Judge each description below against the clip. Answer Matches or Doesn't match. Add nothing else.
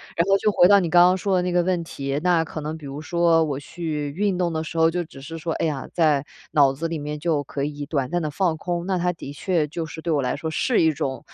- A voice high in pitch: Doesn't match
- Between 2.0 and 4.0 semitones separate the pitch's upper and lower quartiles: Matches